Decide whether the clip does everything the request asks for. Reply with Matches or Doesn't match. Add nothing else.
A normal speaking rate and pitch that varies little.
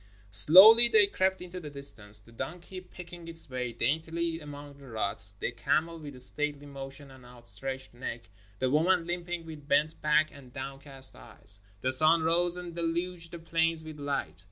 Doesn't match